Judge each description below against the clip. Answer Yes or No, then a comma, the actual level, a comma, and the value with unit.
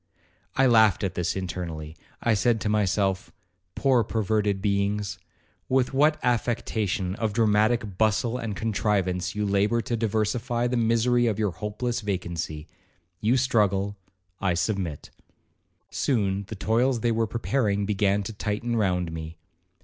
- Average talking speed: No, slow, 130 wpm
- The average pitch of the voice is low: Yes, low, 105 Hz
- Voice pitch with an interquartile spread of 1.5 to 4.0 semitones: Yes, average, 3.2 semitones